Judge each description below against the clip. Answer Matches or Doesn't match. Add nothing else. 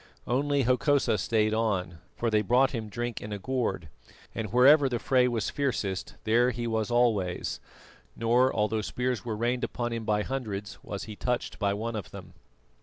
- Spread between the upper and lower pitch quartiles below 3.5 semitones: Matches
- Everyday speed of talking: Matches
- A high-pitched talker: Doesn't match